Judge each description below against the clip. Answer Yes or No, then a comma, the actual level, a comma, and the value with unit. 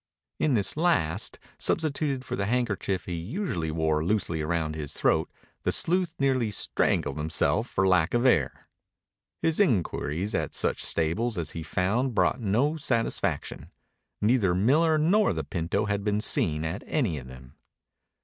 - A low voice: Yes, low, 100 Hz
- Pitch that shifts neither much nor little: No, wide, 8.2 semitones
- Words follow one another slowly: No, average, 150 wpm